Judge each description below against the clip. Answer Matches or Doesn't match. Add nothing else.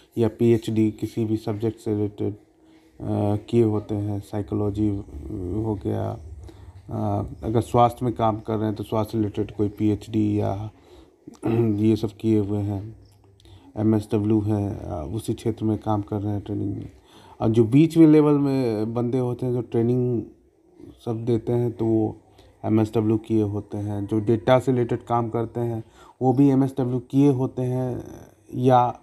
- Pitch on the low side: Matches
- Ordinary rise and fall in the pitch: Doesn't match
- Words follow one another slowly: Doesn't match